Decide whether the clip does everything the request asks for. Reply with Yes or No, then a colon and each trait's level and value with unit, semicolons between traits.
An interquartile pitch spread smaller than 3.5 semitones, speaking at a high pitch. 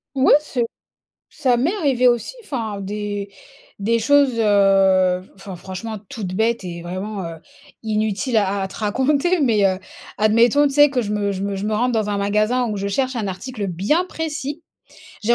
No: average, 4.3 semitones; high, 215 Hz